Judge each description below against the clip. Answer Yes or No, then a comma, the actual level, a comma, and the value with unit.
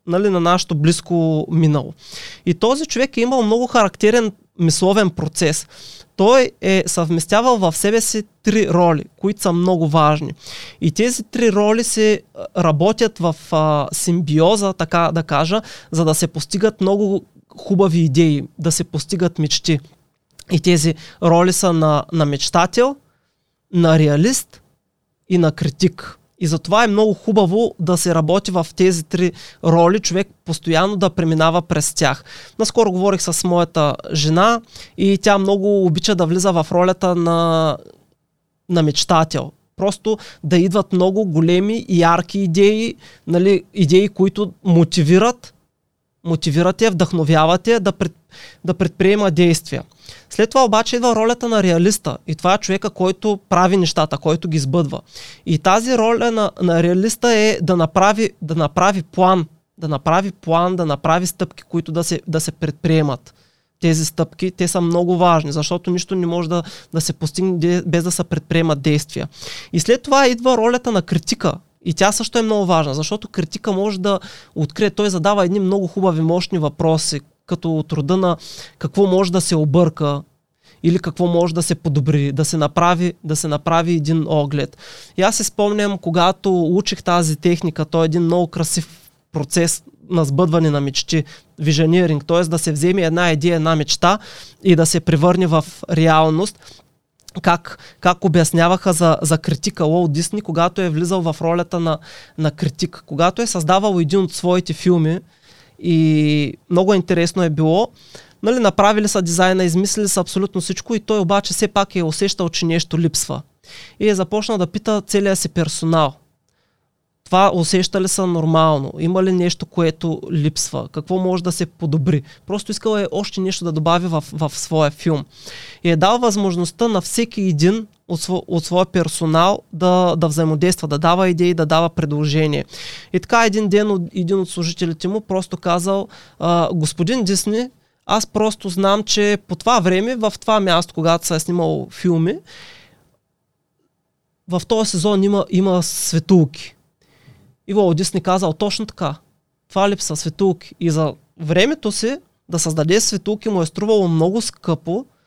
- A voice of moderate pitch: Yes, medium, 175 Hz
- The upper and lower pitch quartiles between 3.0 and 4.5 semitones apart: Yes, average, 3.3 semitones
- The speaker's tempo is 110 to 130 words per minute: No, average, 155 wpm